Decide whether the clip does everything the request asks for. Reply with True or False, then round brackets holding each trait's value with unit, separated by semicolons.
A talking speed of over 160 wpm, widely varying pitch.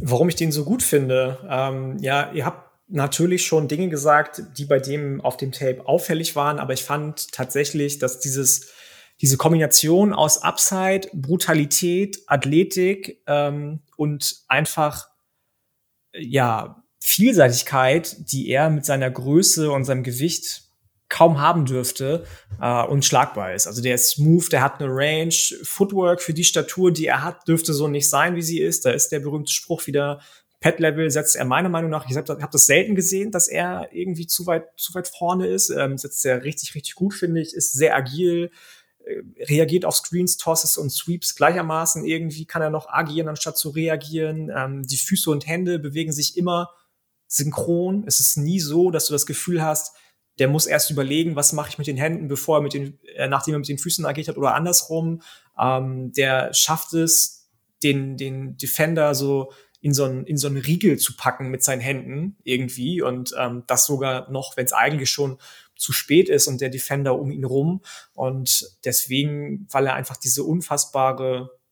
False (180 wpm; 3.5 semitones)